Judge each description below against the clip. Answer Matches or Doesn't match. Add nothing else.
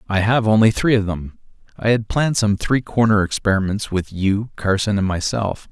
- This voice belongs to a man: Matches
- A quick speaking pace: Doesn't match